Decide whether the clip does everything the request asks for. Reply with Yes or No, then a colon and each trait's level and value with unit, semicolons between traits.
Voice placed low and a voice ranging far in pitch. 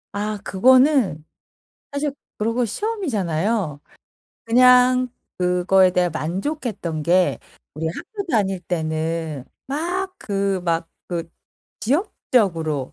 No: high, 195 Hz; wide, 7.1 semitones